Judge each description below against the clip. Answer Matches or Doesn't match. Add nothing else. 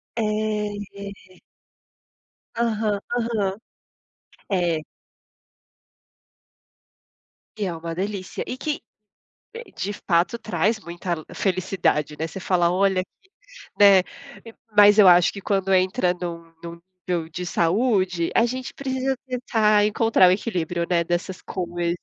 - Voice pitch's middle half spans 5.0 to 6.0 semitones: Doesn't match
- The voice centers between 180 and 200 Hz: Matches